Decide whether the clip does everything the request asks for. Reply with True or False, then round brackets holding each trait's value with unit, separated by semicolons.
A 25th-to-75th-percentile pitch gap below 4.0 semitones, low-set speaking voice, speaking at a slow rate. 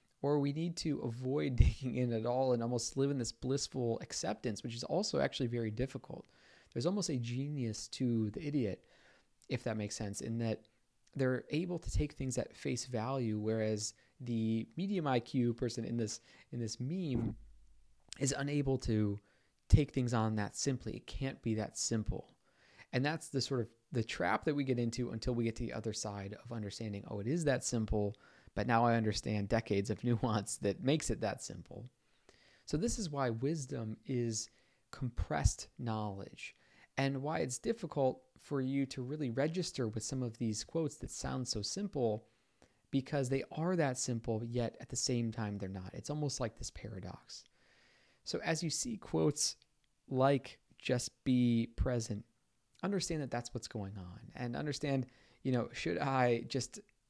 False (3.4 semitones; 125 Hz; 175 wpm)